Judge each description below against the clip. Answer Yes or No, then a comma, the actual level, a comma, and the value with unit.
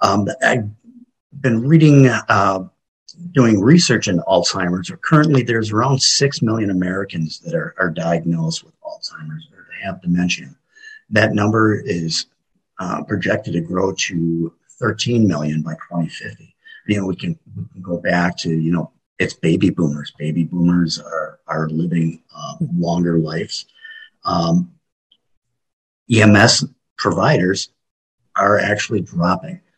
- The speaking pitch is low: Yes, low, 100 Hz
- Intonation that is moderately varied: No, wide, 8.9 semitones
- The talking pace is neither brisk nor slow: No, slow, 125 wpm